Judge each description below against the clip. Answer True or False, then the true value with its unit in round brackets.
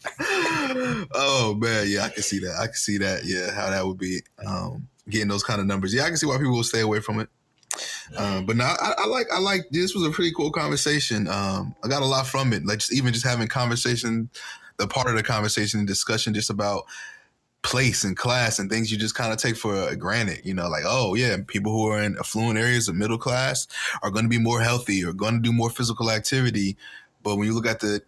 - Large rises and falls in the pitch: False (3.5 semitones)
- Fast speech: True (245 wpm)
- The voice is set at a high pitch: False (115 Hz)